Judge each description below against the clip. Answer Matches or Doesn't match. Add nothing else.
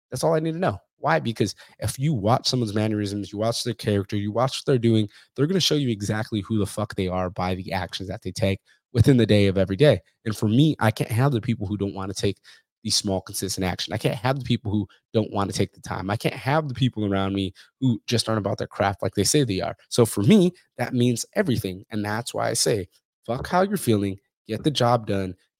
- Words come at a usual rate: Doesn't match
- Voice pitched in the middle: Doesn't match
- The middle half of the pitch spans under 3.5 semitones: Doesn't match